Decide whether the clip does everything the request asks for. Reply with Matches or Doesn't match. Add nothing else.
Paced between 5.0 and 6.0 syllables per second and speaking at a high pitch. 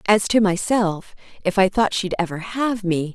Doesn't match